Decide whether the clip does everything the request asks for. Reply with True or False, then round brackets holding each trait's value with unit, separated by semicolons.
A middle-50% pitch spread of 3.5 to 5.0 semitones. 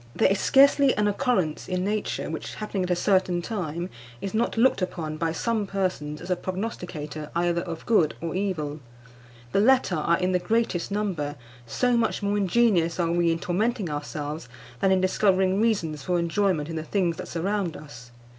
True (3.8 semitones)